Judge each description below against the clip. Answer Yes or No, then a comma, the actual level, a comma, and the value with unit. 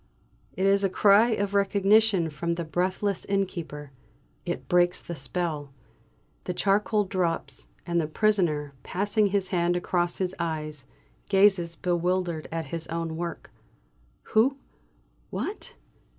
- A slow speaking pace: Yes, slow, 125 wpm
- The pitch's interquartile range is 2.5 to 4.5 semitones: Yes, average, 3.0 semitones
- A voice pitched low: No, medium, 180 Hz